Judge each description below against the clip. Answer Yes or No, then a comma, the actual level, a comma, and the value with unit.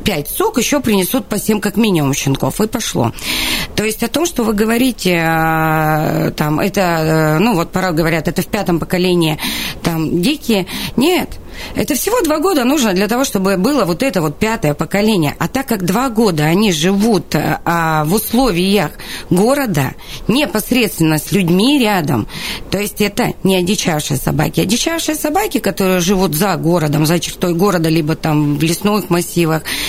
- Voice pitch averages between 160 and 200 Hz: Yes, high, 190 Hz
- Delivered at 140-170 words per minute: Yes, fast, 160 wpm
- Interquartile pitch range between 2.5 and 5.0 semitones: No, wide, 5.6 semitones